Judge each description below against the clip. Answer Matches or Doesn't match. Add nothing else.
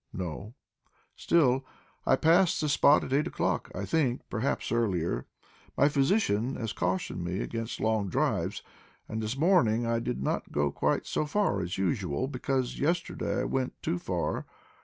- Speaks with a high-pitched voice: Doesn't match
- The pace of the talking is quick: Doesn't match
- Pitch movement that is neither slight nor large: Doesn't match